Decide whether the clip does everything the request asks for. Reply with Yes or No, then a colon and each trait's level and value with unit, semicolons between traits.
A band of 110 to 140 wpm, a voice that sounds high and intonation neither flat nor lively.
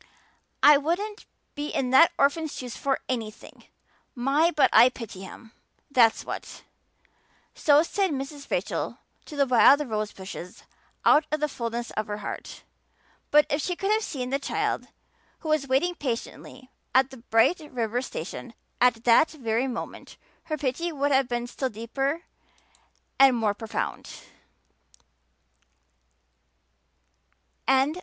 Yes: slow, 135 wpm; very high, 265 Hz; average, 4.2 semitones